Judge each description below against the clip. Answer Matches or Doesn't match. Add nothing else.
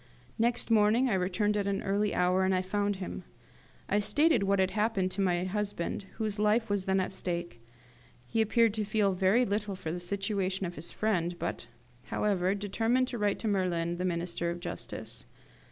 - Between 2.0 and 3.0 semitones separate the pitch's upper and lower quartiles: Matches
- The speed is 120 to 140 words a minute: Doesn't match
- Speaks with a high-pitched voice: Matches